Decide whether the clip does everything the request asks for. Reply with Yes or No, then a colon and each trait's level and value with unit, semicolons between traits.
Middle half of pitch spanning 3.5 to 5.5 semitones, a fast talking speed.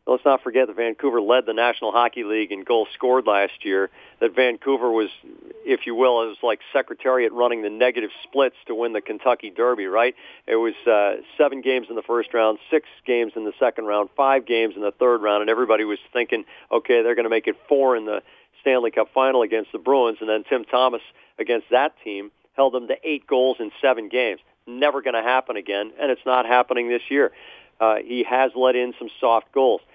No: average, 3.0 semitones; fast, 215 wpm